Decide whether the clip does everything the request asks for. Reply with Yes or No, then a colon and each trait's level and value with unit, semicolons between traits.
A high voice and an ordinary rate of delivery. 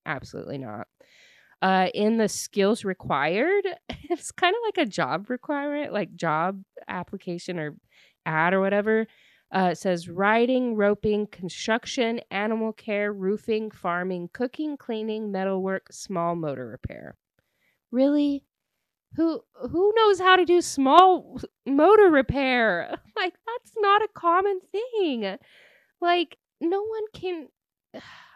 No: high, 225 Hz; slow, 120 wpm